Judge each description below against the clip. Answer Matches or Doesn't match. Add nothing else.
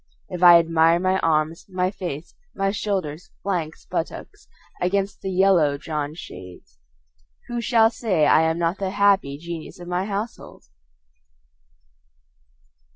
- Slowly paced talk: Matches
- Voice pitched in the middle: Matches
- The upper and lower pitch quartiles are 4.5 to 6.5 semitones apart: Doesn't match